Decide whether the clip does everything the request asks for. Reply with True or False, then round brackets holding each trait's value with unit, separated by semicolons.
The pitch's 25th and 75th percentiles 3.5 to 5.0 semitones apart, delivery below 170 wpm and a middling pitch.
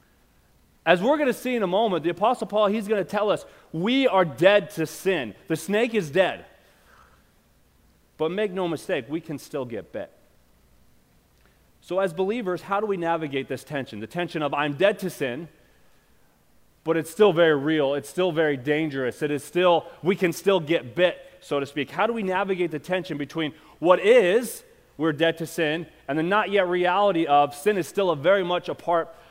False (4.7 semitones; 200 wpm; 170 Hz)